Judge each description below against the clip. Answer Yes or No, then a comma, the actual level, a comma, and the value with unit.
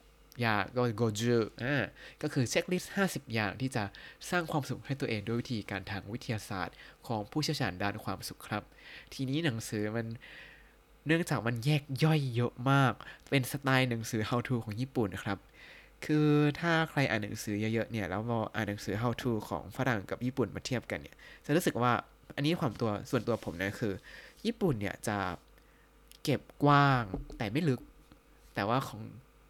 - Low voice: Yes, low, 120 Hz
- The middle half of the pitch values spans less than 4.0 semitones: No, average, 4.9 semitones